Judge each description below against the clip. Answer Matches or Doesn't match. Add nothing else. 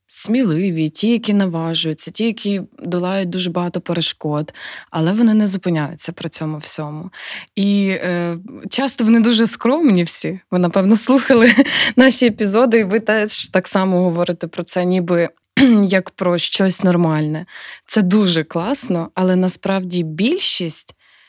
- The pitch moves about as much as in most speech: Matches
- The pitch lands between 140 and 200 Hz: Matches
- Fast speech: Doesn't match